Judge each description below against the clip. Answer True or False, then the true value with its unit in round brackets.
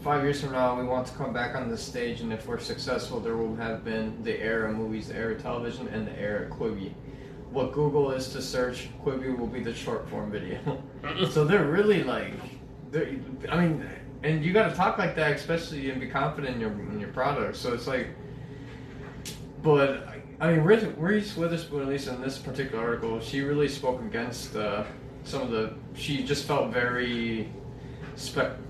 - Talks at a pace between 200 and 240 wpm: False (190 wpm)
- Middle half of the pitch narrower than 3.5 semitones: True (2.7 semitones)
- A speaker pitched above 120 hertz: True (135 Hz)